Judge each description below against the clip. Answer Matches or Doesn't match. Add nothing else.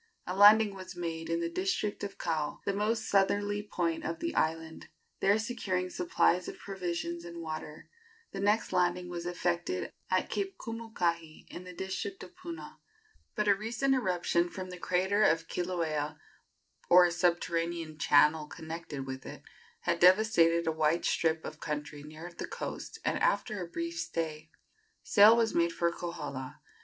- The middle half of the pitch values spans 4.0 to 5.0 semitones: Doesn't match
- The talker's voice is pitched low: Doesn't match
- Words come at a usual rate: Matches